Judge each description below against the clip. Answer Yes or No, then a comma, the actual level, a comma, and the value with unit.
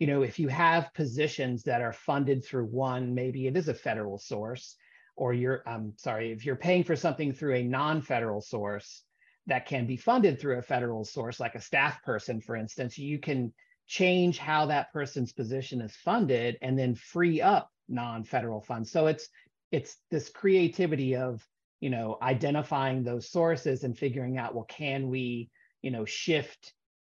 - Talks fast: No, average, 175 wpm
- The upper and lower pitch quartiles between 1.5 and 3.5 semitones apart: No, average, 4.0 semitones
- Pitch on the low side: Yes, low, 130 Hz